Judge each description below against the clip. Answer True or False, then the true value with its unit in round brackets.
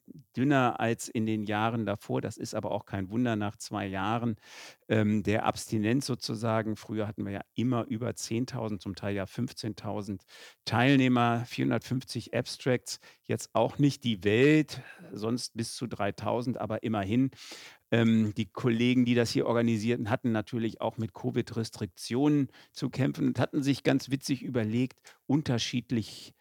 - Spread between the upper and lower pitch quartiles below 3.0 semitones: True (2.5 semitones)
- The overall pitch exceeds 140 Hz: False (115 Hz)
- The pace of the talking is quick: False (150 wpm)